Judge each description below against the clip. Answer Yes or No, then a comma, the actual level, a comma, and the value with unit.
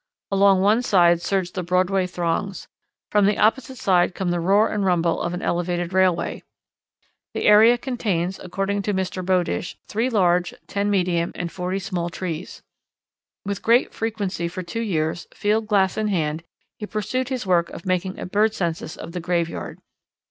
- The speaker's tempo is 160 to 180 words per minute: Yes, average, 170 wpm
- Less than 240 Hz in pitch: Yes, medium, 185 Hz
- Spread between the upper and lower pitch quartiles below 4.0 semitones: Yes, average, 2.9 semitones